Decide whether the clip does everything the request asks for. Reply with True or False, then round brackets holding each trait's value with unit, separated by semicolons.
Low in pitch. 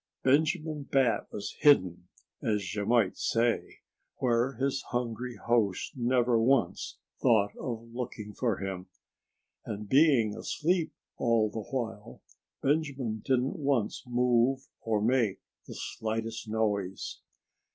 True (115 Hz)